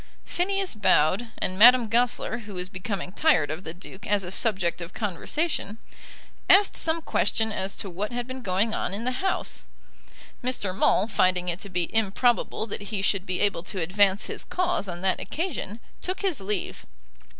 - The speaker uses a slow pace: No, average, 180 wpm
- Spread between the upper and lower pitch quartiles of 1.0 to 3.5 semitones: No, average, 4.8 semitones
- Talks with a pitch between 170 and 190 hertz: No, high, 205 Hz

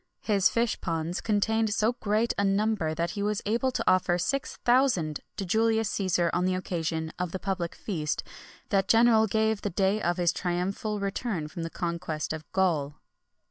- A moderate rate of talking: Yes, average, 180 wpm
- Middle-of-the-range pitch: No, high, 195 Hz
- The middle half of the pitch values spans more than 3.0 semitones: Yes, average, 4.1 semitones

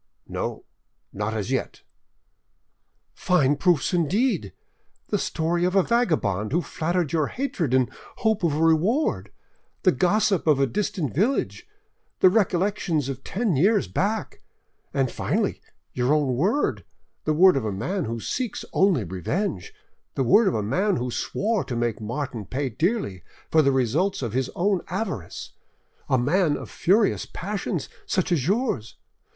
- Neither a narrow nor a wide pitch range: No, wide, 7.4 semitones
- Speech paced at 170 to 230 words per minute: No, average, 150 wpm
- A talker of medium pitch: Yes, medium, 165 Hz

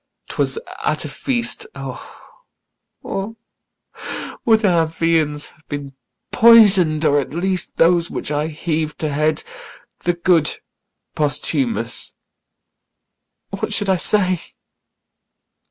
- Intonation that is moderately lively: Yes, average, 4.7 semitones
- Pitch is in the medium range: Yes, medium, 170 Hz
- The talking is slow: Yes, slow, 105 wpm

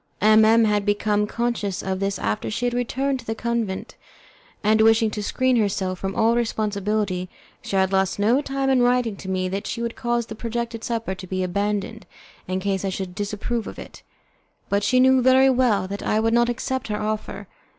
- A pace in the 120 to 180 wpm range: No, average, 200 wpm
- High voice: Yes, high, 215 Hz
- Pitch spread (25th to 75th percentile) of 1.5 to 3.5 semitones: Yes, average, 3.2 semitones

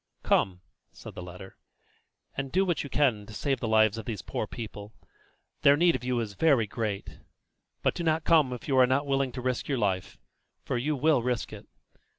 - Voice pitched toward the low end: Yes, low, 125 Hz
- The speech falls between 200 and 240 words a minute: Yes, fast, 205 wpm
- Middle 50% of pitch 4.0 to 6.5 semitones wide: Yes, average, 4.8 semitones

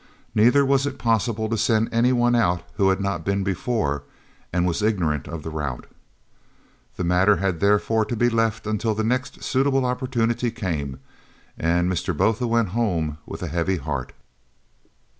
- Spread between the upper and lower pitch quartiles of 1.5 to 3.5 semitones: No, average, 5.1 semitones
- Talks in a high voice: No, low, 105 Hz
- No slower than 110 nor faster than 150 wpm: No, average, 165 wpm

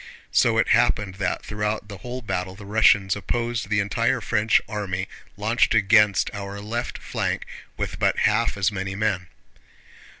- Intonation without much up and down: Yes, narrow, 2.0 semitones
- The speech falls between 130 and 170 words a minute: Yes, average, 155 wpm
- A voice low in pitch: Yes, low, 105 Hz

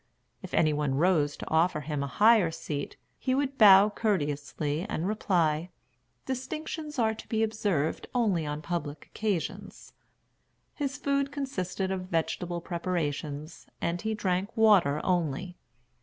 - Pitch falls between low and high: Yes, medium, 180 Hz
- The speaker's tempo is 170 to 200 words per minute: No, slow, 135 wpm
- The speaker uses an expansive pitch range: Yes, wide, 6.0 semitones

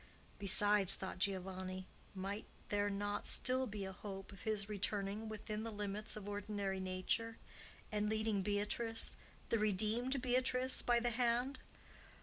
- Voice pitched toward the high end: Yes, high, 210 Hz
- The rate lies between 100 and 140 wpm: Yes, slow, 135 wpm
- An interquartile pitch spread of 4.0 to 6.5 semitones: No, narrow, 2.4 semitones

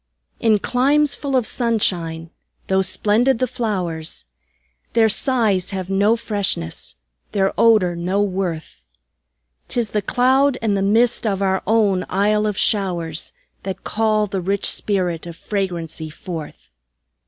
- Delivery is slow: Yes, slow, 130 wpm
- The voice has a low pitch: No, high, 200 Hz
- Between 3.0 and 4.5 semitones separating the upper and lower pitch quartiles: Yes, average, 3.8 semitones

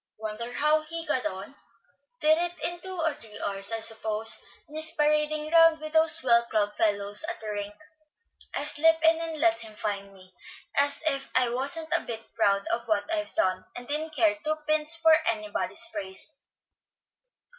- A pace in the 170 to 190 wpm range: Yes, average, 180 wpm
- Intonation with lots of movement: Yes, wide, 6.8 semitones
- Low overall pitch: No, very high, 275 Hz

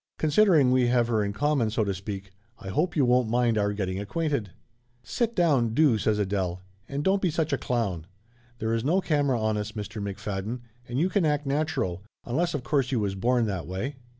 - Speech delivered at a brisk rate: Yes, fast, 210 wpm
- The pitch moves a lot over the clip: Yes, wide, 6.2 semitones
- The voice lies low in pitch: Yes, low, 120 Hz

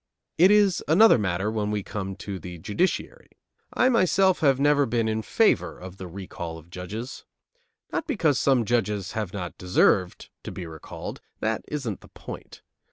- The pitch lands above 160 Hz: No, low, 110 Hz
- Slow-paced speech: No, average, 165 wpm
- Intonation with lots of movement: Yes, wide, 7.7 semitones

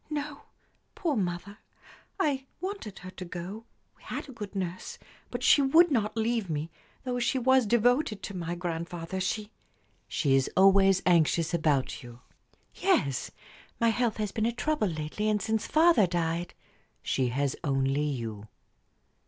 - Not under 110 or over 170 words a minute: Yes, average, 160 wpm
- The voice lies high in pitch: Yes, high, 195 Hz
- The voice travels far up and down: Yes, wide, 6.4 semitones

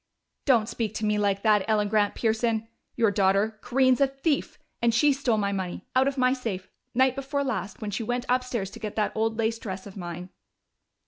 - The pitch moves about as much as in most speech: Yes, average, 3.8 semitones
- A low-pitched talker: No, high, 220 Hz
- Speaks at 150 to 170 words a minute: No, fast, 205 wpm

